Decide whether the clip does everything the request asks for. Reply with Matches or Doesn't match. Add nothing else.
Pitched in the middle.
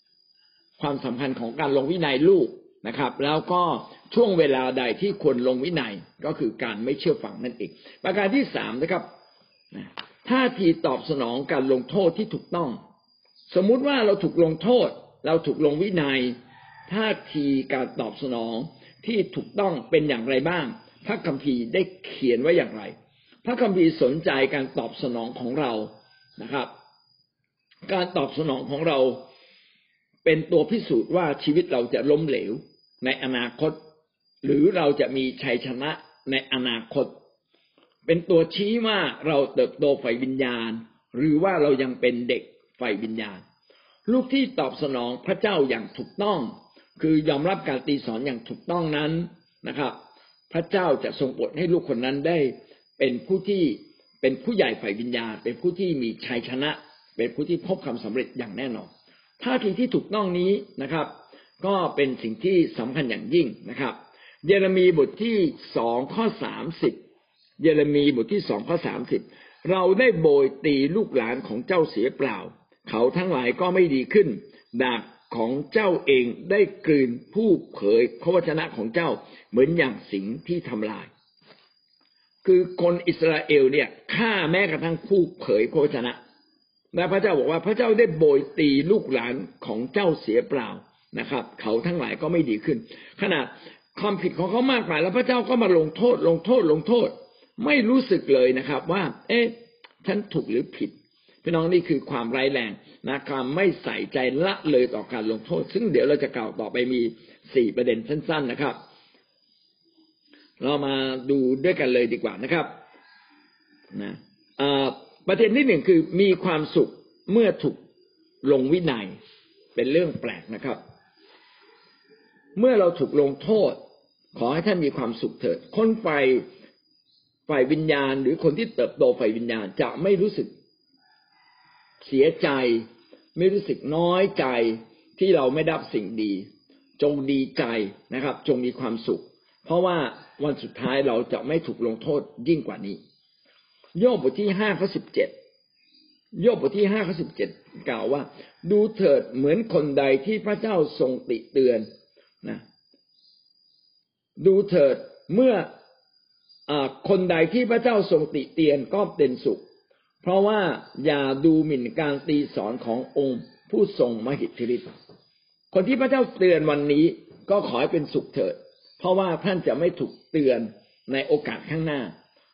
Matches